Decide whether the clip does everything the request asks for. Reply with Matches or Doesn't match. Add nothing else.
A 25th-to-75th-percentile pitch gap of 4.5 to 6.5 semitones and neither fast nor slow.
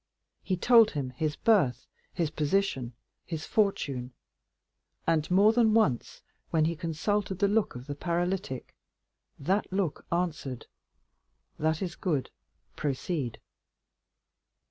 Doesn't match